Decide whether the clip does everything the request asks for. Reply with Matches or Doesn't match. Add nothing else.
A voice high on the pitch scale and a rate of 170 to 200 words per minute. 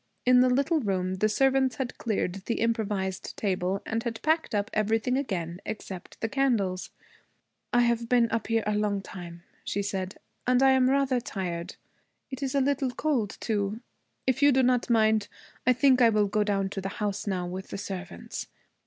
Matches